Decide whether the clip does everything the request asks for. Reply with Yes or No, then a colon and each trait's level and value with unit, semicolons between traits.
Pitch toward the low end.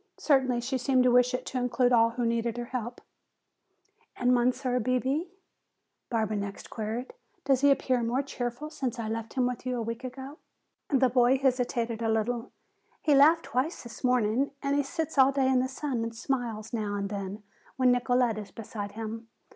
No: high, 245 Hz